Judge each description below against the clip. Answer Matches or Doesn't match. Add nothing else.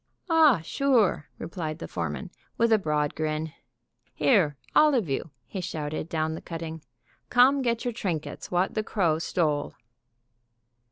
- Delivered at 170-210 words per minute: Doesn't match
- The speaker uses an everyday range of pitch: Doesn't match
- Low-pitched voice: Doesn't match